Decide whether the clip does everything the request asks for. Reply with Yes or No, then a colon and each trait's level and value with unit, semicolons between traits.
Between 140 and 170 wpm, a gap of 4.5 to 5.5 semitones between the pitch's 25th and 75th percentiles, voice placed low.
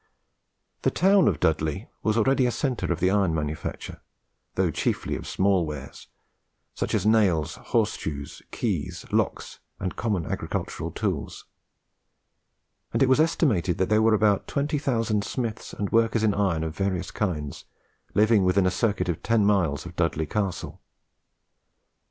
Yes: average, 150 wpm; average, 4.9 semitones; low, 100 Hz